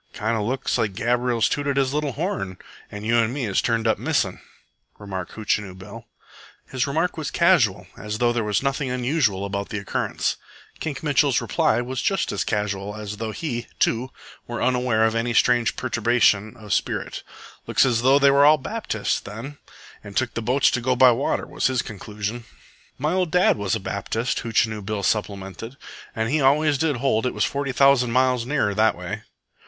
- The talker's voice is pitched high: No, low, 120 Hz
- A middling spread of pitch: Yes, average, 4.1 semitones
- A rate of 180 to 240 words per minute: Yes, average, 185 wpm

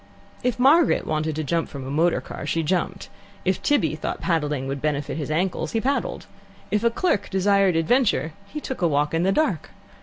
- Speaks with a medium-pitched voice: Yes, medium, 170 Hz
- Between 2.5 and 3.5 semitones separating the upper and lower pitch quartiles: No, wide, 5.5 semitones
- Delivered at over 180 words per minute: Yes, average, 195 wpm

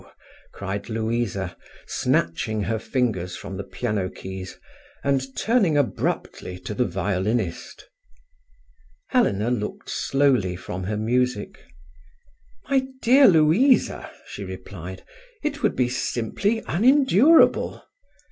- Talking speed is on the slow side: Yes, slow, 100 wpm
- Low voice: Yes, low, 115 Hz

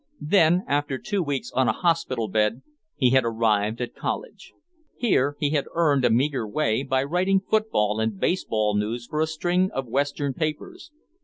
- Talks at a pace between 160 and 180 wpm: Yes, average, 170 wpm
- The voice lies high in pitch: No, medium, 140 Hz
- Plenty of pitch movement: Yes, wide, 6.3 semitones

